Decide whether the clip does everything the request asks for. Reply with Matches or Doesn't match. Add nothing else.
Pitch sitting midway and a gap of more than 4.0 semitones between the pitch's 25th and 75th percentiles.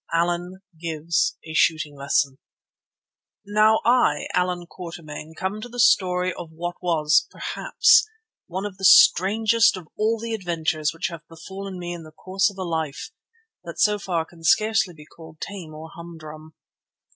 Doesn't match